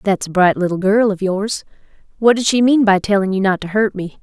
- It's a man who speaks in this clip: No, female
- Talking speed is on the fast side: Yes, fast, 240 wpm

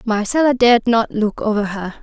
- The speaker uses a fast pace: No, average, 175 wpm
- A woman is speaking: Yes, female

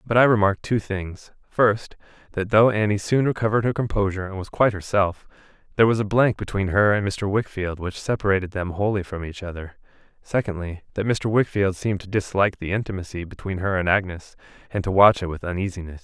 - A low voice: Yes, low, 100 Hz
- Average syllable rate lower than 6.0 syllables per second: No, 6.1 syllables/s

